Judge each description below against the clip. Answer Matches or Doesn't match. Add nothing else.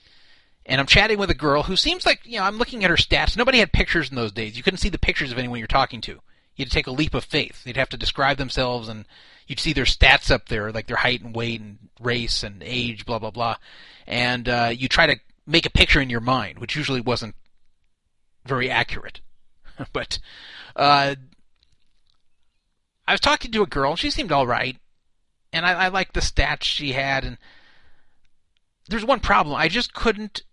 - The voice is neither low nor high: Doesn't match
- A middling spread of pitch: Doesn't match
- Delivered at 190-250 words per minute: Matches